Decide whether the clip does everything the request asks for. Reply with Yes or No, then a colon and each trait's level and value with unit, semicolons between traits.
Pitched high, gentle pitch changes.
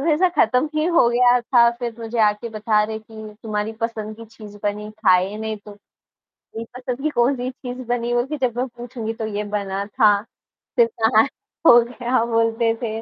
Yes: high, 230 Hz; narrow, 2.3 semitones